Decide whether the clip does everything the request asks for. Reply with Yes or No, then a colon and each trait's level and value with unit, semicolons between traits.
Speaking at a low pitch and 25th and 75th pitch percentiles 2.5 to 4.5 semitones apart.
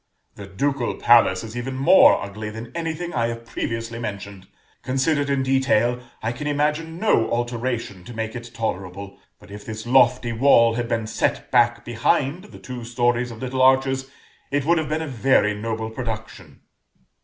Yes: low, 120 Hz; average, 3.0 semitones